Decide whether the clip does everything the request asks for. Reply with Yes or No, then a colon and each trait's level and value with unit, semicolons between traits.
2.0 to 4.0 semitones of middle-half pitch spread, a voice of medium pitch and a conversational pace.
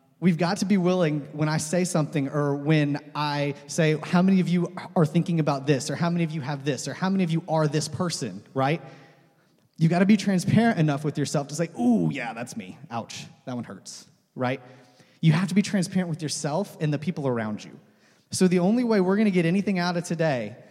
No: average, 3.7 semitones; medium, 160 Hz; fast, 230 wpm